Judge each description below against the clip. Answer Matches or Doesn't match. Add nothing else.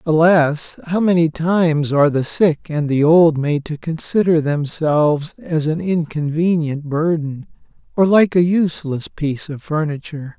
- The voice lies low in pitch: Doesn't match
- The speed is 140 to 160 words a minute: Matches